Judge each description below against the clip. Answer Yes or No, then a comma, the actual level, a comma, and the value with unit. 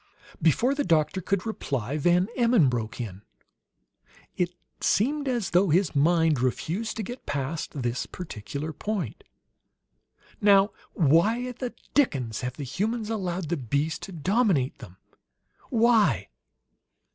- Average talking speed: No, slow, 125 wpm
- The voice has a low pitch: No, medium, 175 Hz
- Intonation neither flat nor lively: No, wide, 7.6 semitones